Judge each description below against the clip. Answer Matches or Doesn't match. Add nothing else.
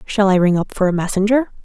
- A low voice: Doesn't match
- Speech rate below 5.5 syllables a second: Doesn't match